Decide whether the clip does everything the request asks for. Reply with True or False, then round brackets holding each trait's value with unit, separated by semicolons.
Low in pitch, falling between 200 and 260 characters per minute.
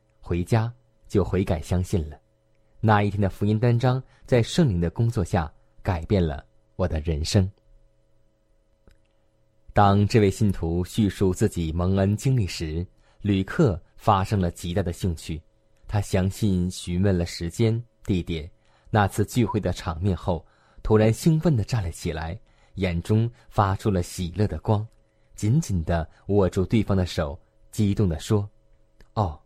True (105 Hz; 210 characters per minute)